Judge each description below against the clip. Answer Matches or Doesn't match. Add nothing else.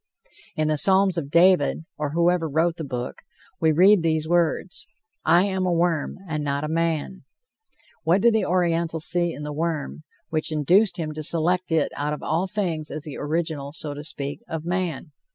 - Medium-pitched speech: Matches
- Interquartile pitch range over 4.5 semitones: Doesn't match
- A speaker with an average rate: Matches